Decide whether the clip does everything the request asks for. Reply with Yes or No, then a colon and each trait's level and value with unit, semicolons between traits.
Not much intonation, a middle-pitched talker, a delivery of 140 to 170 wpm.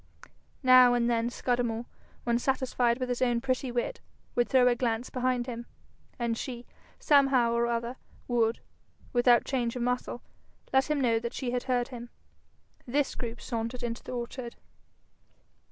No: narrow, 1.3 semitones; high, 245 Hz; average, 155 wpm